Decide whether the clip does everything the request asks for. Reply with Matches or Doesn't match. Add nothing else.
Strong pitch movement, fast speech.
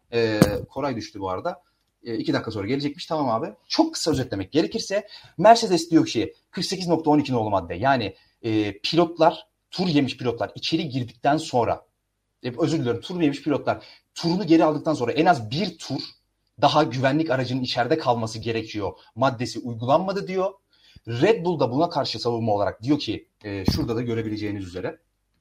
Matches